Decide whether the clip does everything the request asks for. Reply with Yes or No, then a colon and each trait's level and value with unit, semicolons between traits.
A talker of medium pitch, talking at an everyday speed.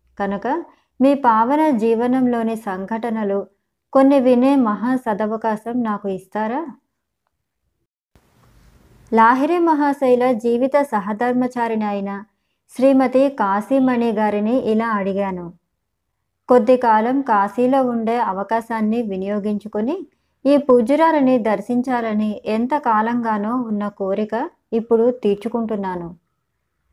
No: high, 230 Hz; average, 80 wpm